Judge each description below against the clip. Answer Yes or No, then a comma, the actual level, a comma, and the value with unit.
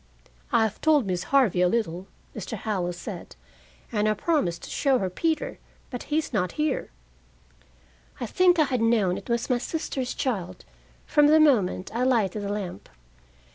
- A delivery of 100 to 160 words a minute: No, average, 175 wpm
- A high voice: Yes, high, 230 Hz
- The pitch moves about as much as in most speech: No, wide, 6.7 semitones